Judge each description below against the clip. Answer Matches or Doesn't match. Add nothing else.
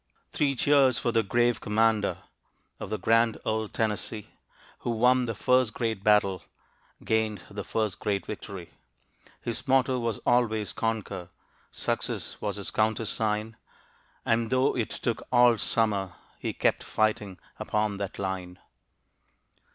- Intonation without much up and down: Matches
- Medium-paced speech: Doesn't match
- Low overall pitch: Matches